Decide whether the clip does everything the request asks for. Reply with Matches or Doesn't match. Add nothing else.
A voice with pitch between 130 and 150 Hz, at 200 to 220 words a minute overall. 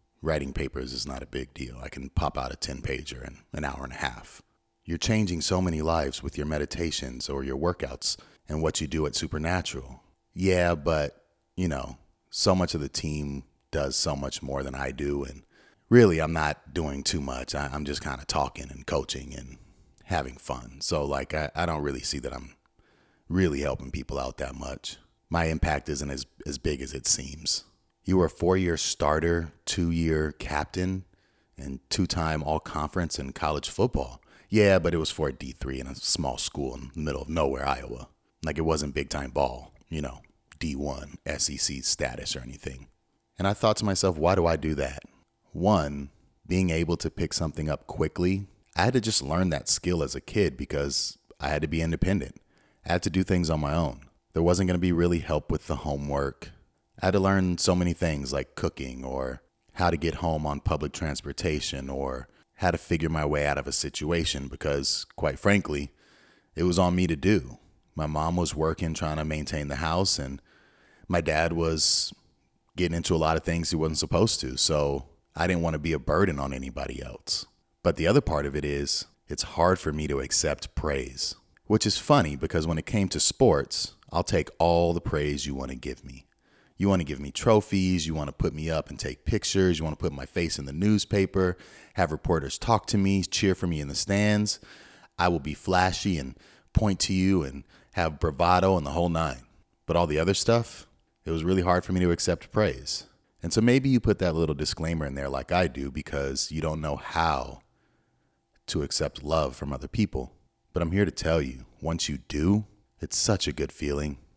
Doesn't match